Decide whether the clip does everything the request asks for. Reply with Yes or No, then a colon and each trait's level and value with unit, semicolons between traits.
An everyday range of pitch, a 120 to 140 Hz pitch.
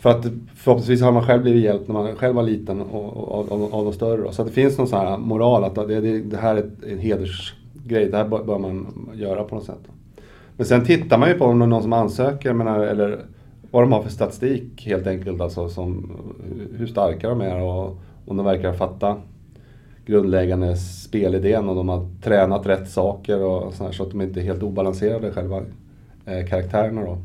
No: average, 3.5 semitones; low, 105 Hz